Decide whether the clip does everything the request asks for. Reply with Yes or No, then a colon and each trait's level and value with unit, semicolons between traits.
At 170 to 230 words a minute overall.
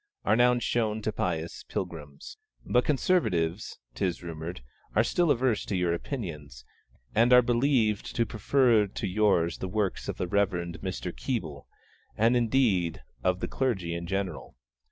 No: average, 155 wpm